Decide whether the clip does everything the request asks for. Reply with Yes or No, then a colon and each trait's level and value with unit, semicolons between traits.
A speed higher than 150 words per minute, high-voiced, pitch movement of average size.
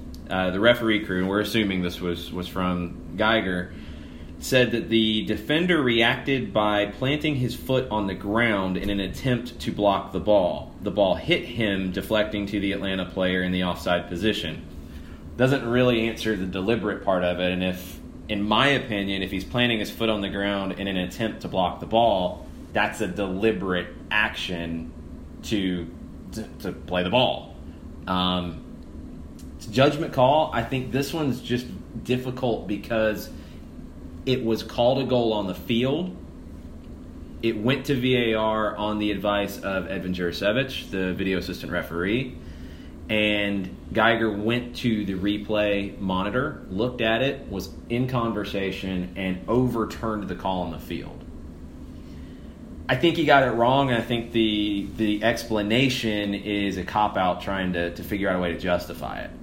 No: average, 165 wpm; low, 100 Hz; average, 4.2 semitones